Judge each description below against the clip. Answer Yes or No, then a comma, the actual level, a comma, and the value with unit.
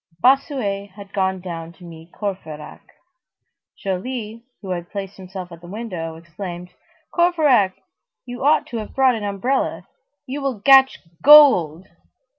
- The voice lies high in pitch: Yes, high, 200 Hz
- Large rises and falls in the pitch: Yes, wide, 6.2 semitones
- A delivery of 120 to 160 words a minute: Yes, slow, 135 wpm